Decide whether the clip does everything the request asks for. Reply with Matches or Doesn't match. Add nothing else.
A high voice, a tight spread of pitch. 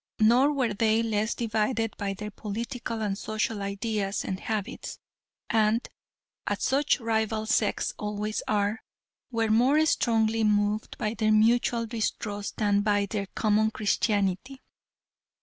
Matches